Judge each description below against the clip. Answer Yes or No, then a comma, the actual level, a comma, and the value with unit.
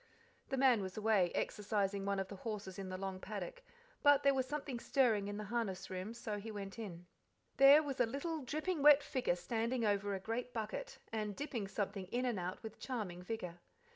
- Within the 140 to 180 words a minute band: No, average, 200 wpm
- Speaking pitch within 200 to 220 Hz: Yes, high, 215 Hz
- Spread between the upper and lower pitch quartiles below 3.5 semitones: No, average, 4.7 semitones